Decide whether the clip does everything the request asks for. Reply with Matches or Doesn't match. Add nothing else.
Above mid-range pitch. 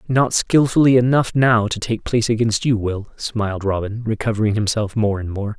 Doesn't match